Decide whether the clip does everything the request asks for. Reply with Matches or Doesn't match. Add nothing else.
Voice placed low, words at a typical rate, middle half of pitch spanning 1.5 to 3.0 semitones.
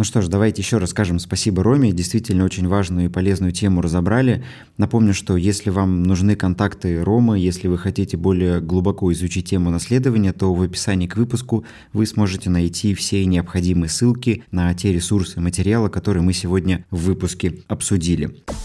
Doesn't match